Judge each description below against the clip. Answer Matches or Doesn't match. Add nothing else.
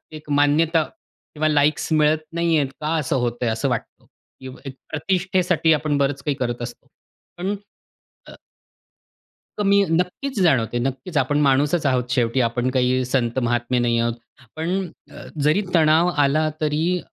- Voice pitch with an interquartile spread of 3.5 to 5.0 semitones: Matches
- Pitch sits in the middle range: Matches